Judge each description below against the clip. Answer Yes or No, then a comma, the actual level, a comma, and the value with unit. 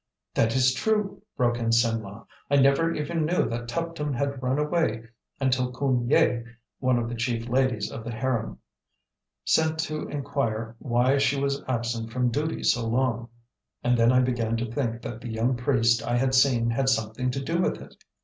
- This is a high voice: No, low, 125 Hz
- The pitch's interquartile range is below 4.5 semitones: Yes, average, 3.0 semitones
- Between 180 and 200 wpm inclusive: Yes, average, 185 wpm